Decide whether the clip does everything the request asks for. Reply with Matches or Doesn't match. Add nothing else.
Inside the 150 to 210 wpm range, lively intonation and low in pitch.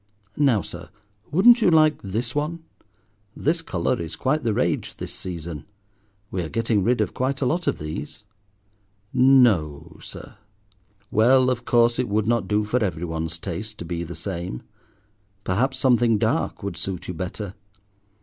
Matches